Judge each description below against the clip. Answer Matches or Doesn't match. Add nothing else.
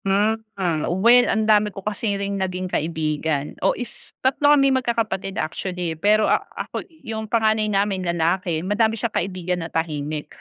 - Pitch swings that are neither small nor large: Matches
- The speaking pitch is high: Matches